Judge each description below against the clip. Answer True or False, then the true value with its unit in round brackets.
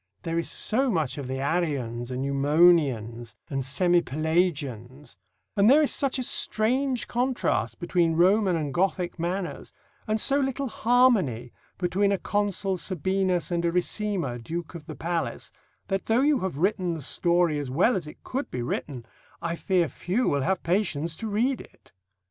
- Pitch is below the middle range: False (175 Hz)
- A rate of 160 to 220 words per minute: True (165 wpm)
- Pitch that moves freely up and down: True (6.0 semitones)